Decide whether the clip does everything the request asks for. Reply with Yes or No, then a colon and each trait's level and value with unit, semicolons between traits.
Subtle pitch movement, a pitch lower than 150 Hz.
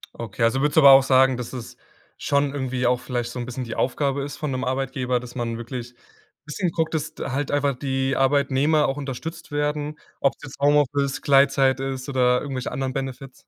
Yes: narrow, 2.2 semitones; low, 135 Hz